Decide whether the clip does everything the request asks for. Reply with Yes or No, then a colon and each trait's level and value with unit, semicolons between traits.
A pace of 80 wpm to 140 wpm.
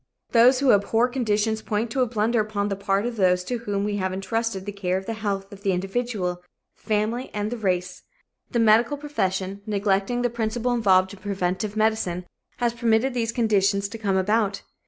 No: average, 190 wpm